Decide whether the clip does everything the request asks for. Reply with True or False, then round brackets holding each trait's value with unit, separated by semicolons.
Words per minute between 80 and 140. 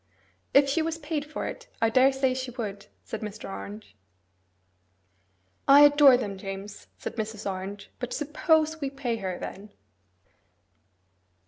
True (135 wpm)